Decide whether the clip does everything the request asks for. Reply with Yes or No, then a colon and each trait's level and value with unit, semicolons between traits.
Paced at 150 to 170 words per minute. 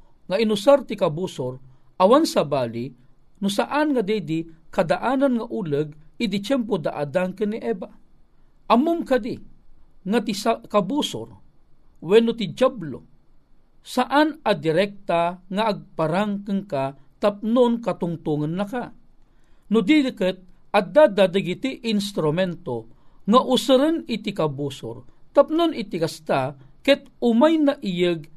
No: average, 115 wpm